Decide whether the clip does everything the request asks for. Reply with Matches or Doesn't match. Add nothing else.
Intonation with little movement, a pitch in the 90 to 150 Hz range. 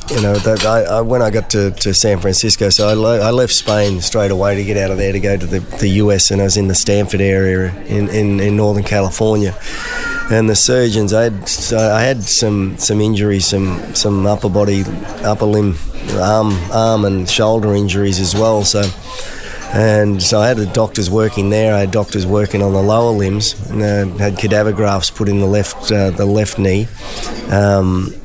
Matches